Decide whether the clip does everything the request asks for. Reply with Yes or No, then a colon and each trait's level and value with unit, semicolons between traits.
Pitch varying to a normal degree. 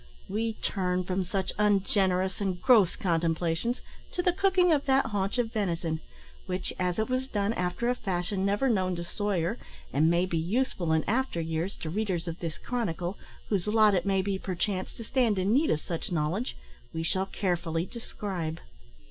Yes: average, 4.1 semitones